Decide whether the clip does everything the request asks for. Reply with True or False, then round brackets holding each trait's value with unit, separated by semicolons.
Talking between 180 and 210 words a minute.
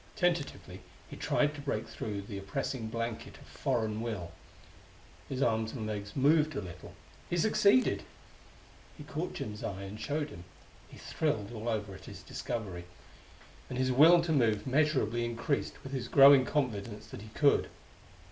False (160 wpm)